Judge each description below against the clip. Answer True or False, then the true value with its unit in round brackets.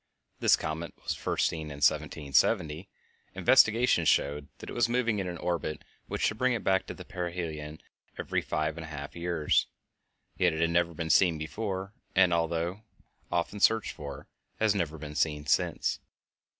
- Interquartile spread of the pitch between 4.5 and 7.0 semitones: False (3.8 semitones)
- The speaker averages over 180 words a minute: False (165 wpm)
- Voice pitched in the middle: False (85 Hz)